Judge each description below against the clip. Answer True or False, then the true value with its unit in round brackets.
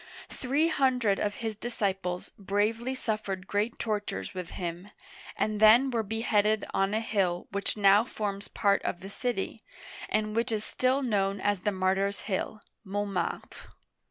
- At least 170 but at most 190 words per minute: False (145 wpm)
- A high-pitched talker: True (205 Hz)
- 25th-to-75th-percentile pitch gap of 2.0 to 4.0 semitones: True (2.4 semitones)